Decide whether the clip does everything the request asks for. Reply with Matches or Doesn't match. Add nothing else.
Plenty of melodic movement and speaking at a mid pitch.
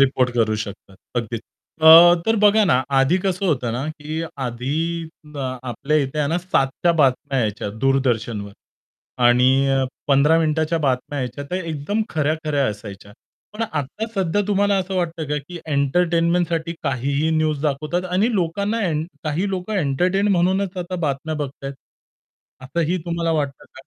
Doesn't match